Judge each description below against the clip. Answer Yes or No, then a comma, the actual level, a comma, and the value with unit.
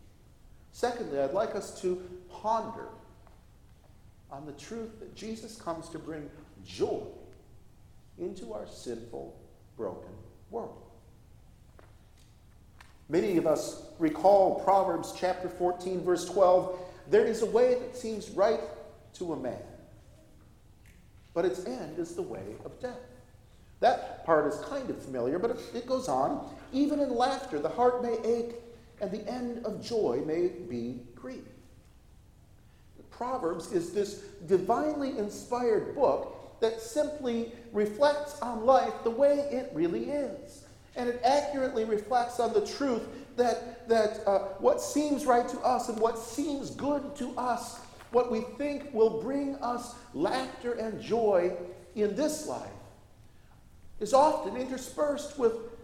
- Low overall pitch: No, high, 225 Hz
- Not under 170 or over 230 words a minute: No, slow, 135 wpm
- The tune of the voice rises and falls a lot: Yes, wide, 5.9 semitones